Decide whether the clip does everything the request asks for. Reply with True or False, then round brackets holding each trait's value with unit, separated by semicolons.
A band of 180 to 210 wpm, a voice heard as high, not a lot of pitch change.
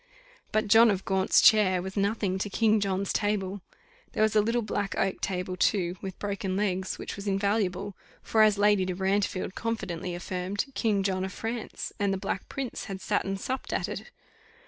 True (190 wpm; 200 Hz; 2.0 semitones)